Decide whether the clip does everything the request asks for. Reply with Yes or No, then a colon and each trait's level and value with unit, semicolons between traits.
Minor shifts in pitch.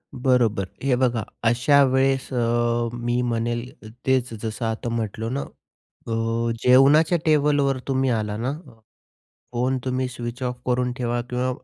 Yes: narrow, 2.0 semitones